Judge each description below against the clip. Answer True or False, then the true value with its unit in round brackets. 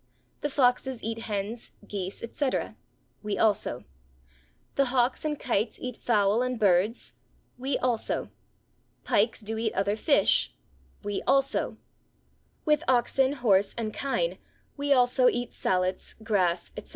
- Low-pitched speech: False (235 Hz)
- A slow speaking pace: True (125 wpm)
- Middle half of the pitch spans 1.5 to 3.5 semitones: False (4.1 semitones)